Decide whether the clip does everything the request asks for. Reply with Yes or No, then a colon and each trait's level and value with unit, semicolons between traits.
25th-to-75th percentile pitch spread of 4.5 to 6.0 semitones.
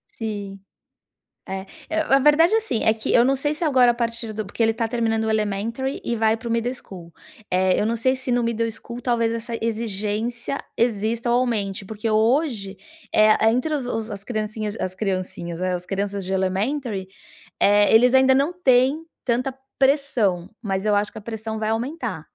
No: average, 3.4 semitones